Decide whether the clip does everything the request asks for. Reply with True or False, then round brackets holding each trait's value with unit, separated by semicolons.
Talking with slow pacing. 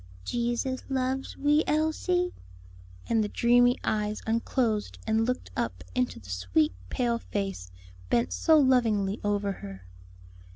True (125 wpm)